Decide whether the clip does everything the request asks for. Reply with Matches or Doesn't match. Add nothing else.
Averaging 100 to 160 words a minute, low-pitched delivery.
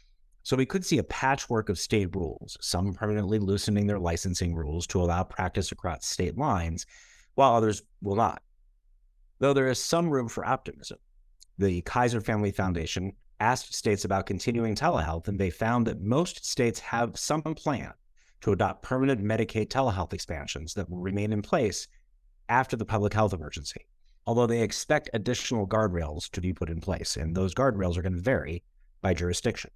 Doesn't match